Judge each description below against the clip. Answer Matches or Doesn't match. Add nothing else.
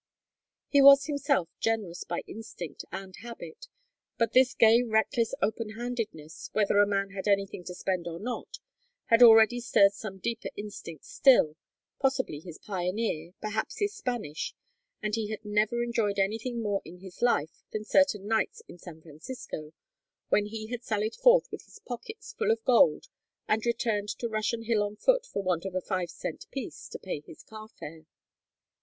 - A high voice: Matches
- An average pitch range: Matches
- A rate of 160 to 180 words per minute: Matches